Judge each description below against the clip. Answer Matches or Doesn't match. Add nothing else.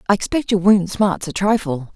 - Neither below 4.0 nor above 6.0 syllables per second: Matches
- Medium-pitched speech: Doesn't match